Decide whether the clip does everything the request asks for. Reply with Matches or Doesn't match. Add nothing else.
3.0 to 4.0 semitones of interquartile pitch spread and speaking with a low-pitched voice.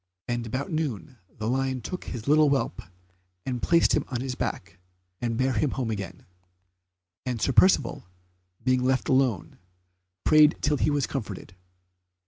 Matches